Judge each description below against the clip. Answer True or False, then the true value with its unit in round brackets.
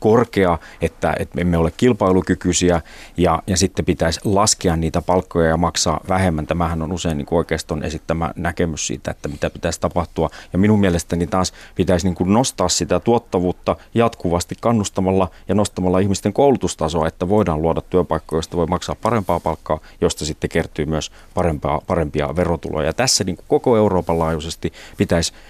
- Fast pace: True (160 wpm)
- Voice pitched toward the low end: True (85 Hz)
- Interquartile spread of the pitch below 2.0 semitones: False (2.5 semitones)